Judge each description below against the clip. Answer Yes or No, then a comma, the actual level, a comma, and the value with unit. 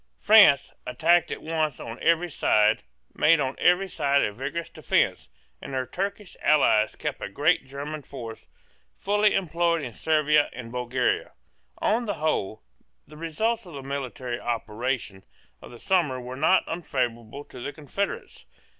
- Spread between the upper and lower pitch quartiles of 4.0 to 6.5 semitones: Yes, average, 5.2 semitones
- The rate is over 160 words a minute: No, average, 150 wpm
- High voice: No, medium, 145 Hz